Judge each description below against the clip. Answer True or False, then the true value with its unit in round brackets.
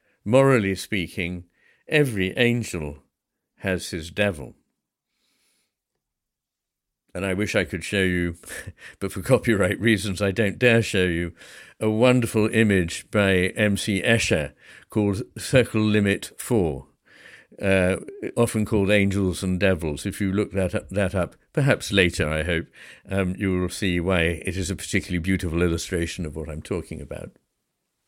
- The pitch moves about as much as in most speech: True (3.1 semitones)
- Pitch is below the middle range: True (95 Hz)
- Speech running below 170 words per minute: True (140 wpm)